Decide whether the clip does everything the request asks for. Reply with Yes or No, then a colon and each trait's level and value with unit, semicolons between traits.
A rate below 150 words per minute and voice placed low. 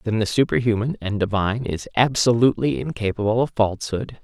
Yes: average, 140 wpm; low, 115 Hz